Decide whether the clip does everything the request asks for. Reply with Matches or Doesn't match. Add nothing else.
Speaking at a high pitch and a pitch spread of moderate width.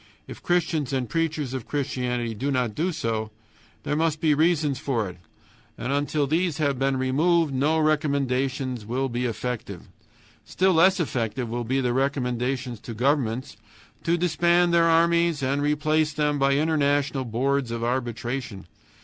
Doesn't match